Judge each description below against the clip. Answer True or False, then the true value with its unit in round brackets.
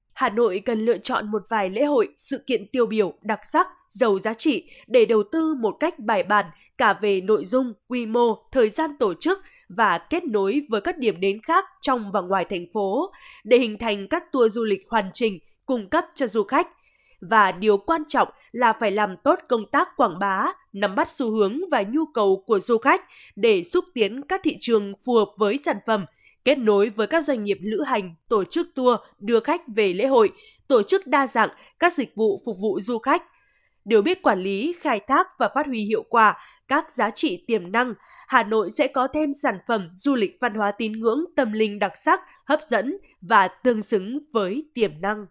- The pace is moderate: True (215 wpm)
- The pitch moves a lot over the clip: True (7.0 semitones)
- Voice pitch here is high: True (245 Hz)